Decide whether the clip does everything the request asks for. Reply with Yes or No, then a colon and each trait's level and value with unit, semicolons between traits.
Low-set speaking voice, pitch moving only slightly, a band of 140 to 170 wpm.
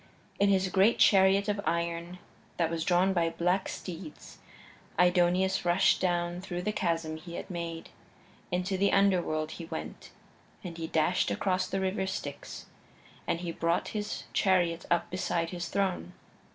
No: medium, 180 Hz; narrow, 2.2 semitones; average, 150 wpm